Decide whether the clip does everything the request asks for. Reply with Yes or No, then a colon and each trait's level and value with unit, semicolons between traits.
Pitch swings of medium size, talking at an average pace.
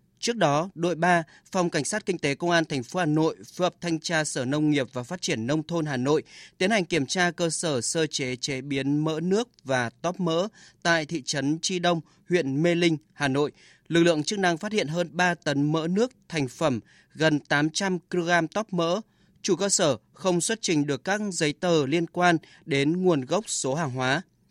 Yes: average, 3.4 semitones; average, 220 wpm